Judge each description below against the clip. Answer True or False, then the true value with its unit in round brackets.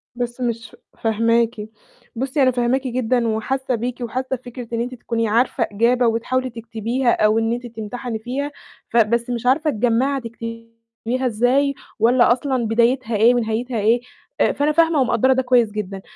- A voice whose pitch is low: False (240 Hz)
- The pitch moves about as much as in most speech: False (2.0 semitones)